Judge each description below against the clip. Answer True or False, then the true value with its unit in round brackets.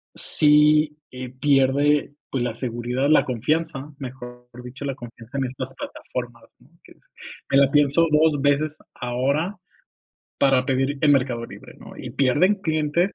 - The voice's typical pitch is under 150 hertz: True (135 Hz)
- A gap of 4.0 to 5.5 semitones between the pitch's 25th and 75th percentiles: False (2.9 semitones)